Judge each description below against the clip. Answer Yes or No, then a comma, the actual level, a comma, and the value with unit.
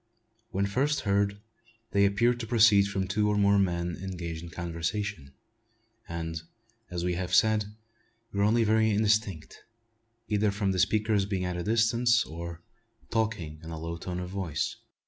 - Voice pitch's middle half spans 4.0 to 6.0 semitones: No, average, 3.6 semitones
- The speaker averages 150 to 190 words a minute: Yes, average, 160 wpm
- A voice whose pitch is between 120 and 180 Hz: No, low, 100 Hz